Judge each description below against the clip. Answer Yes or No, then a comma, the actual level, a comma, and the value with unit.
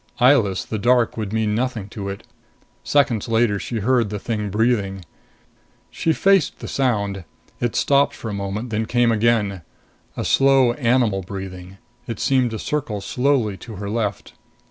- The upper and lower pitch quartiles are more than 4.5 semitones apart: No, average, 3.7 semitones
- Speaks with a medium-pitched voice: No, low, 110 Hz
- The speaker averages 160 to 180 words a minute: Yes, average, 165 wpm